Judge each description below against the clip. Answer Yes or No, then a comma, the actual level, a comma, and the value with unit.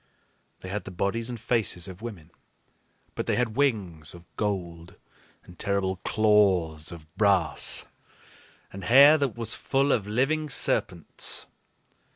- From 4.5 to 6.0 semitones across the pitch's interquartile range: Yes, average, 4.9 semitones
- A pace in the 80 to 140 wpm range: Yes, slow, 135 wpm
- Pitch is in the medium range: No, low, 100 Hz